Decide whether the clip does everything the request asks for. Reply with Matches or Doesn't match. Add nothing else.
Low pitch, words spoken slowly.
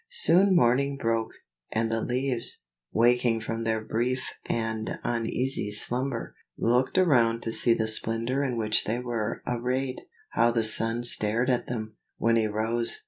Doesn't match